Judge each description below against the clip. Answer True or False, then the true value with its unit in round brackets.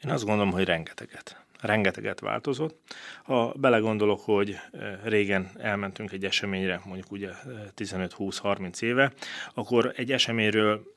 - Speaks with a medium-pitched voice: False (105 Hz)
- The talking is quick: False (115 wpm)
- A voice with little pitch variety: False (3.1 semitones)